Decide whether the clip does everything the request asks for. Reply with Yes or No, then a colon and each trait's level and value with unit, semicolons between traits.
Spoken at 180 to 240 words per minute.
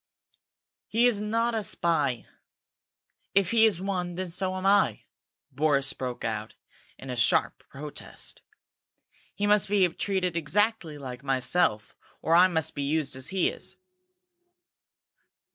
No: slow, 135 wpm